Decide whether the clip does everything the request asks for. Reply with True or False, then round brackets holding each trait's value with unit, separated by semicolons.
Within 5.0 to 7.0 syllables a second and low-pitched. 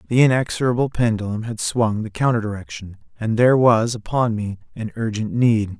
True (5.4 syllables/s; 110 Hz)